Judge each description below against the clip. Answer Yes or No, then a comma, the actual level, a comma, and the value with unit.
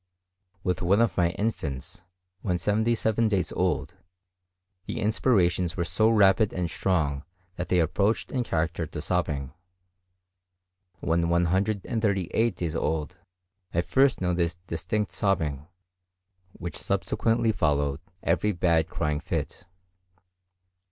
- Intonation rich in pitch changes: No, average, 4.3 semitones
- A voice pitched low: Yes, very low, 90 Hz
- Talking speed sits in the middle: No, slow, 115 wpm